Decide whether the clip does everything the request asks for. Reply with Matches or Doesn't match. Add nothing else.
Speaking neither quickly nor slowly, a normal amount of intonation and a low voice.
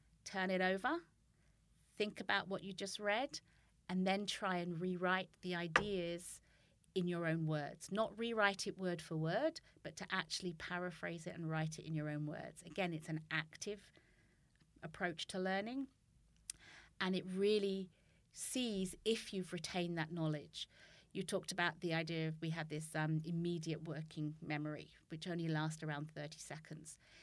Doesn't match